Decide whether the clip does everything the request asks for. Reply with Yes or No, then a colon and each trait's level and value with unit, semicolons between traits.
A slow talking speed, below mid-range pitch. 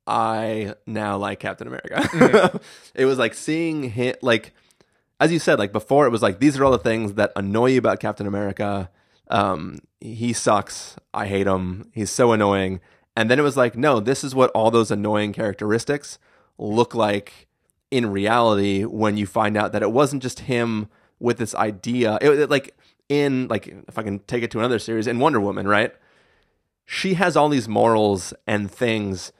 No: average, 190 wpm; low, 110 Hz